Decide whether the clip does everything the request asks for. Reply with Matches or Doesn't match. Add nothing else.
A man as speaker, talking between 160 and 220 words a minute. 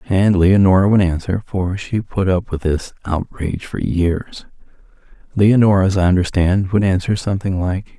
Doesn't match